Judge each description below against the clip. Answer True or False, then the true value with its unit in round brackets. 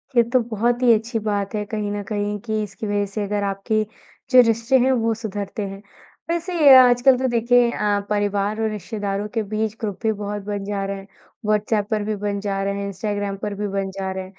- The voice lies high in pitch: True (210 Hz)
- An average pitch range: False (2.0 semitones)